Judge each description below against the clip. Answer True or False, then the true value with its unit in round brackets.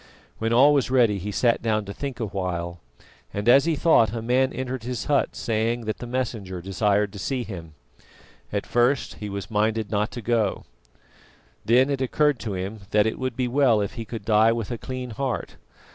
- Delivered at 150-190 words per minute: False (205 wpm)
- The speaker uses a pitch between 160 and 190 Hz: False (115 Hz)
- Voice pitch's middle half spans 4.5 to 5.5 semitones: False (3.5 semitones)